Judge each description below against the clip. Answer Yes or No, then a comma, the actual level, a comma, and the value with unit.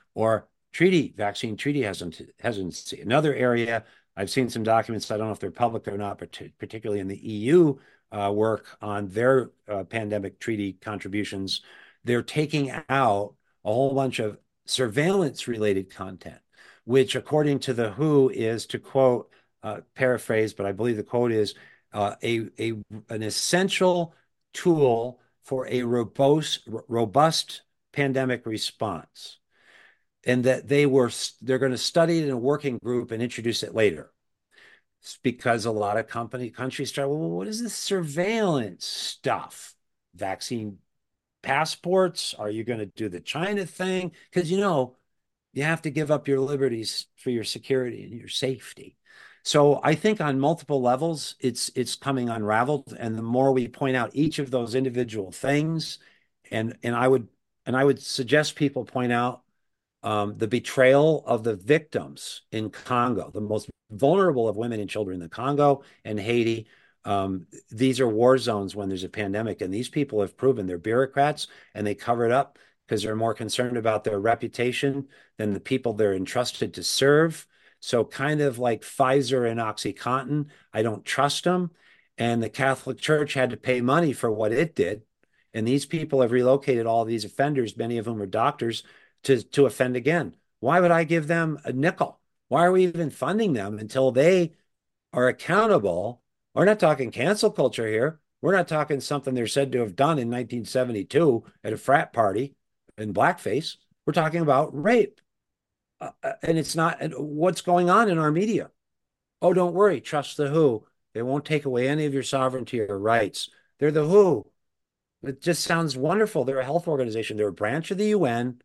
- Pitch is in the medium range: No, low, 130 Hz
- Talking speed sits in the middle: Yes, average, 175 wpm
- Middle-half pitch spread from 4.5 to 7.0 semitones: Yes, average, 4.8 semitones